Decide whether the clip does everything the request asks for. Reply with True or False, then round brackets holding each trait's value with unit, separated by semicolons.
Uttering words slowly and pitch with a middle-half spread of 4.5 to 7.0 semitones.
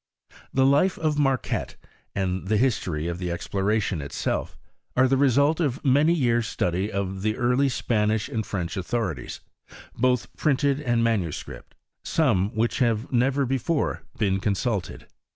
False (145 wpm; 5.6 semitones)